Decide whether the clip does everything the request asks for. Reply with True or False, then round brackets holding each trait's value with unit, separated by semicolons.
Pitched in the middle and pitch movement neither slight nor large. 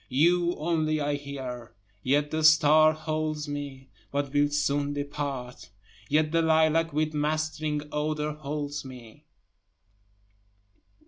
False (150 Hz; 1.5 semitones)